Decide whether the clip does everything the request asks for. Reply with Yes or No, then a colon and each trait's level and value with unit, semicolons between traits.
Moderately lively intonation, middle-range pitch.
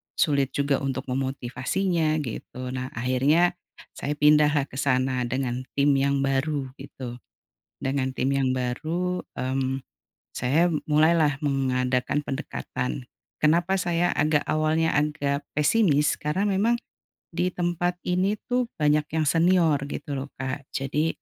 Yes: average, 3.6 semitones; medium, 145 Hz